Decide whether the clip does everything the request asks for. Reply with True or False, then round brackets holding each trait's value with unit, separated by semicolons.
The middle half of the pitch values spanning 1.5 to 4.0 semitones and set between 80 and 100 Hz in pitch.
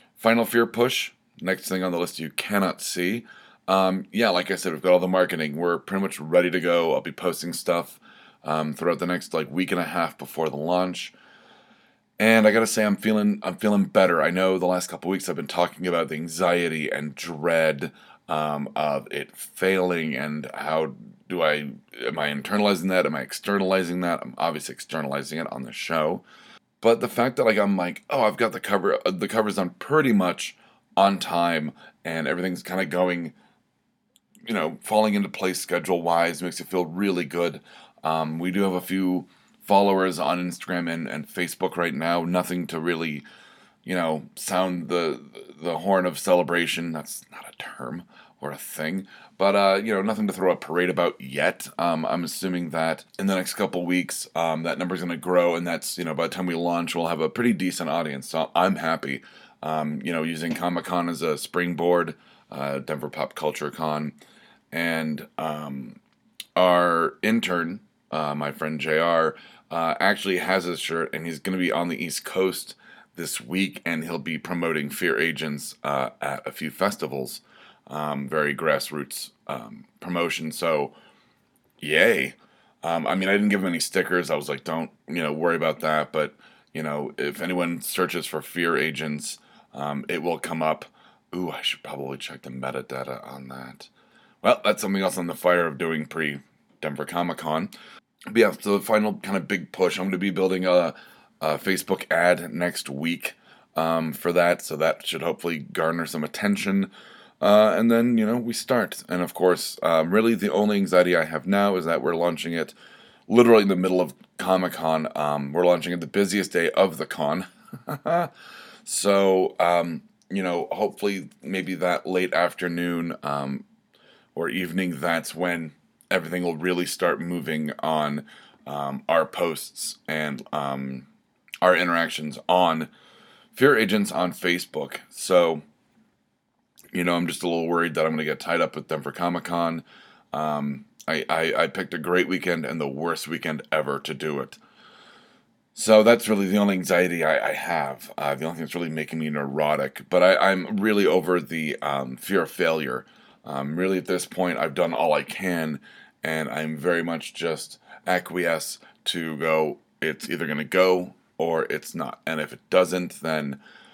True (2.9 semitones; 85 Hz)